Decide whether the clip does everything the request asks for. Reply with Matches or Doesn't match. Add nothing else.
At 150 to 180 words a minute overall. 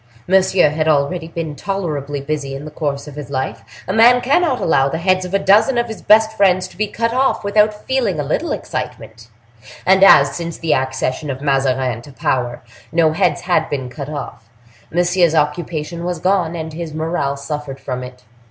Doesn't match